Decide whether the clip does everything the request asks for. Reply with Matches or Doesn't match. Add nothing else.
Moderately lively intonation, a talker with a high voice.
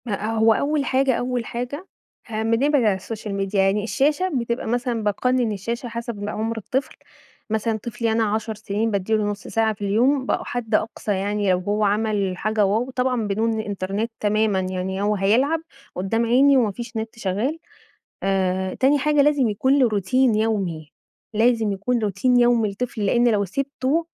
Matches